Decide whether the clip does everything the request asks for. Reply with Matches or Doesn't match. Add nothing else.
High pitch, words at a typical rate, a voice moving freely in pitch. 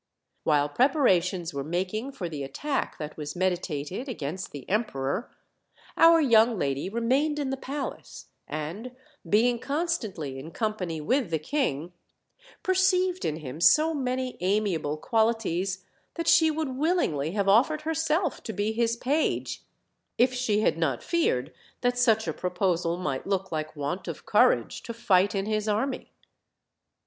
Matches